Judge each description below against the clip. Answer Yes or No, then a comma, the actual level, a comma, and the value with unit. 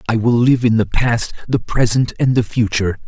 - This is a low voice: Yes, low, 115 Hz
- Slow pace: No, fast, 215 wpm